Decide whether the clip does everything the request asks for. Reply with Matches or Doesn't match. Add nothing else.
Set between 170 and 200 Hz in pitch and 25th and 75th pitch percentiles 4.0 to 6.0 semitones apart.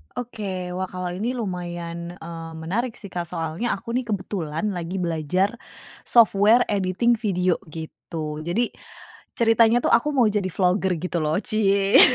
Matches